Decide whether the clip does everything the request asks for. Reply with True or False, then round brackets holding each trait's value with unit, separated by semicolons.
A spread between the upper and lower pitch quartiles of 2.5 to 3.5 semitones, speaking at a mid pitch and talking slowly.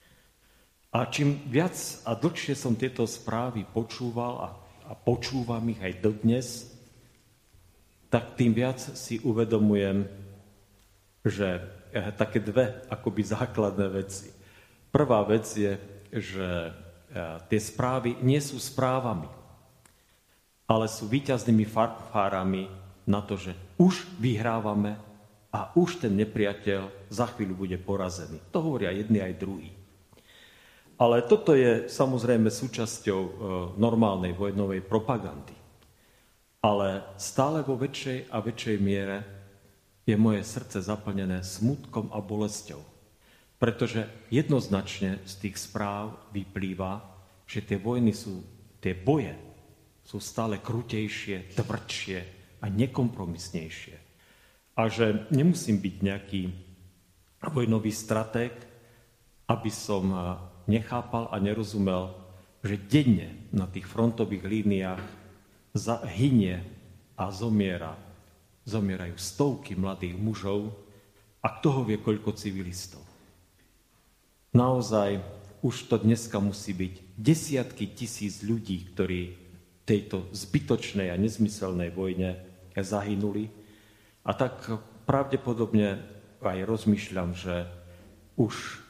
False (3.2 semitones; 105 Hz; 100 wpm)